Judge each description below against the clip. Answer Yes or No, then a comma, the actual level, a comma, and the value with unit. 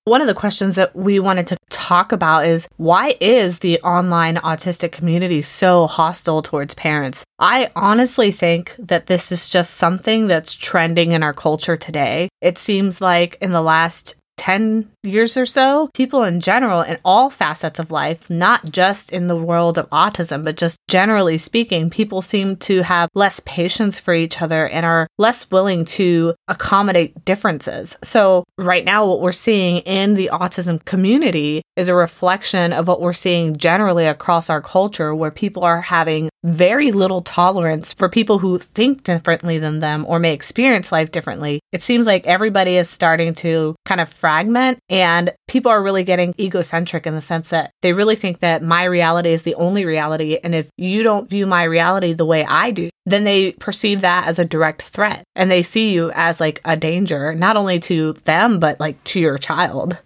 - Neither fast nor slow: Yes, average, 185 wpm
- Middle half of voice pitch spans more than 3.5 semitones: No, average, 2.9 semitones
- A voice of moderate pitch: Yes, medium, 175 Hz